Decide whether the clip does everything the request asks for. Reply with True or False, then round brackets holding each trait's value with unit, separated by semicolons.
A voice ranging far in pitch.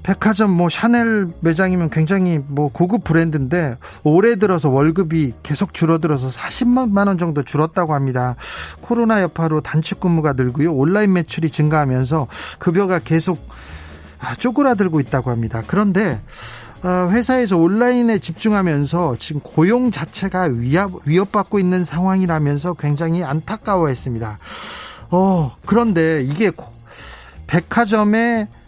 False (5.0 semitones)